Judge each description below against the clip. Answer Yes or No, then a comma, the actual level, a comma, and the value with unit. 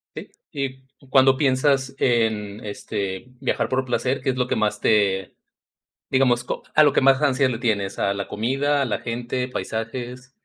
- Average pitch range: Yes, average, 3.2 semitones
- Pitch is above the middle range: No, low, 125 Hz